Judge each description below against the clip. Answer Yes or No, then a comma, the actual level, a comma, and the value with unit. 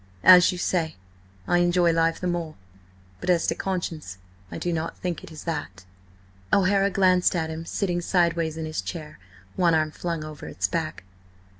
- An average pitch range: No, narrow, 2.3 semitones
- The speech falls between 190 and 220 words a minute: No, average, 170 wpm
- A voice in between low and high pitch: Yes, medium, 165 Hz